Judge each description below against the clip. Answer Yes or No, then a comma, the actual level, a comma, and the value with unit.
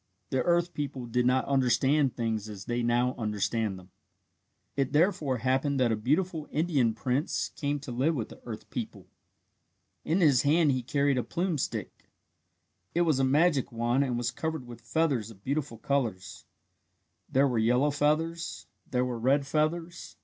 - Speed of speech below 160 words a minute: No, average, 165 wpm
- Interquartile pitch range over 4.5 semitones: No, average, 4.1 semitones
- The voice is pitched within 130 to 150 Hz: Yes, low, 135 Hz